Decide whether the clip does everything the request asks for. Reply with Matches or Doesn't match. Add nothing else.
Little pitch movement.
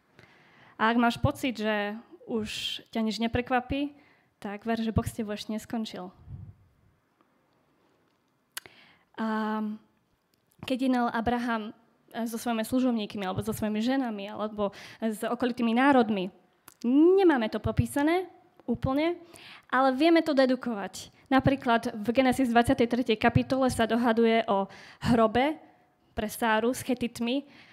Doesn't match